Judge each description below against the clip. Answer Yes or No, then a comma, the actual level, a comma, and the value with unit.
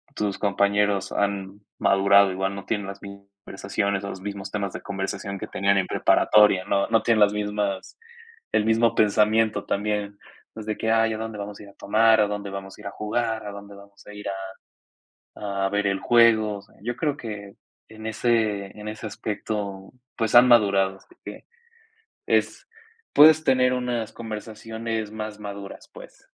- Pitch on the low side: Yes, low, 105 Hz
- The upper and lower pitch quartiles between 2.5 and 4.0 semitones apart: No, narrow, 1.9 semitones